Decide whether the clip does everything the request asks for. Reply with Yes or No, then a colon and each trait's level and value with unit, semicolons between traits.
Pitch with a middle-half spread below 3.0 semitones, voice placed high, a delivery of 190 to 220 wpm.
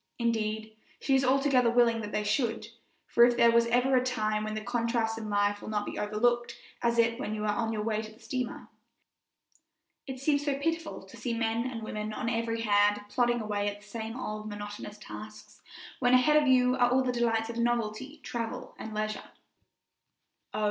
Yes: narrow, 2.5 semitones; high, 230 Hz; average, 200 wpm